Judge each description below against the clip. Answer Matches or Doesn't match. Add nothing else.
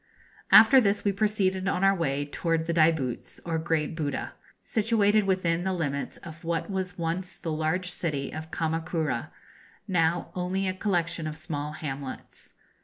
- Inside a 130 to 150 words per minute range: Doesn't match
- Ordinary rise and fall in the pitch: Matches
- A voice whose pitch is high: Doesn't match